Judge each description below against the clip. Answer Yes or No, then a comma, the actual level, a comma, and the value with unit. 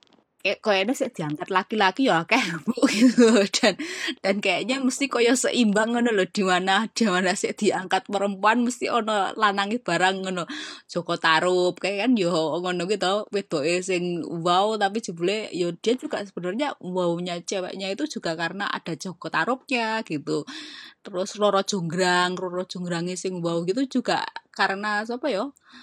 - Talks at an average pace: No, fast, 160 wpm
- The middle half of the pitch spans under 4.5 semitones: Yes, average, 3.9 semitones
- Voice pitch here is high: Yes, high, 195 Hz